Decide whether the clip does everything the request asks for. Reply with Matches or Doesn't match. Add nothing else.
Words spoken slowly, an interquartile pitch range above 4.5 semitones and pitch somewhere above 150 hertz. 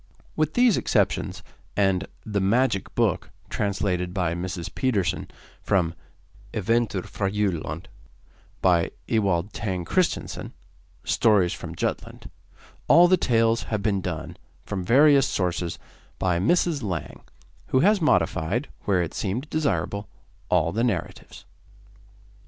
Doesn't match